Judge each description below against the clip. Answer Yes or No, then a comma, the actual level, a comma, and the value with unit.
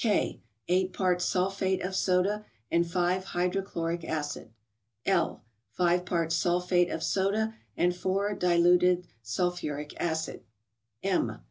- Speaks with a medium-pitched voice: Yes, medium, 180 Hz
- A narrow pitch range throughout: Yes, narrow, 1.7 semitones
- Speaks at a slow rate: Yes, slow, 120 wpm